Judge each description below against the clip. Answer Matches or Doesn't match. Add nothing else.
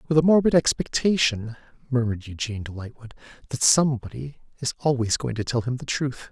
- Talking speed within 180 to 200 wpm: Doesn't match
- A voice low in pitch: Matches